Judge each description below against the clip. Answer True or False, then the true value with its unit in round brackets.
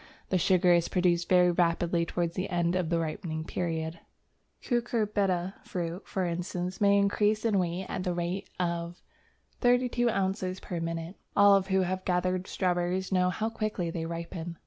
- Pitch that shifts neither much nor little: False (2.1 semitones)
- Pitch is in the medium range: True (180 Hz)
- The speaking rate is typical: True (160 wpm)